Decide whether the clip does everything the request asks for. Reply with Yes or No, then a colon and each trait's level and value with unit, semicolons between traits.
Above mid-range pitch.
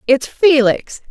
Yes: very high, 275 Hz